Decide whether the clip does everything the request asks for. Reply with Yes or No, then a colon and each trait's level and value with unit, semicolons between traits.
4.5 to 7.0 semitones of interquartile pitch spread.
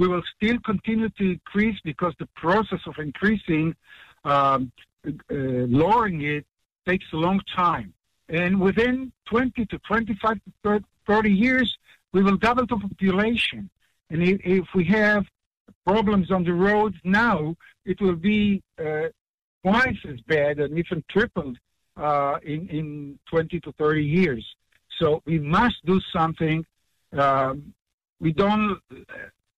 Yes: average, 5.0 semitones